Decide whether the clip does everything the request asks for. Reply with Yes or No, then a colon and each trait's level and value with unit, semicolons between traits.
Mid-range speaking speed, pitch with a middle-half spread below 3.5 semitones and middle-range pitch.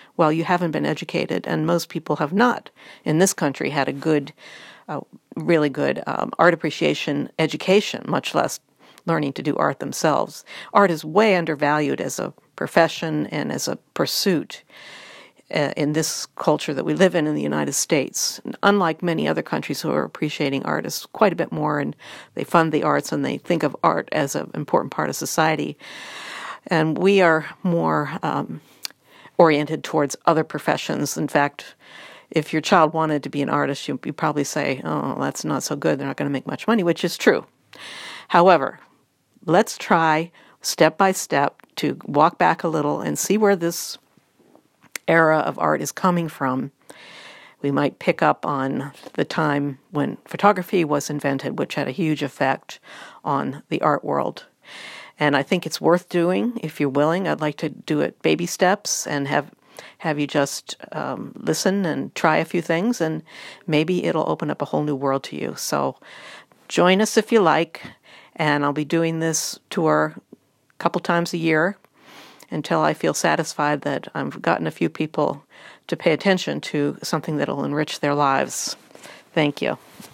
Yes: average, 175 wpm; average, 2.8 semitones; medium, 160 Hz